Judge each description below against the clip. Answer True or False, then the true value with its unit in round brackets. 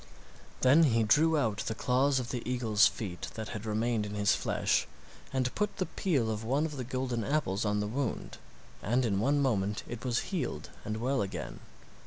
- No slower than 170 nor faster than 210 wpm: True (195 wpm)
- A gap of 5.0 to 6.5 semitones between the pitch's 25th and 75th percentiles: False (4.2 semitones)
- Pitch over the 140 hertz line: False (120 Hz)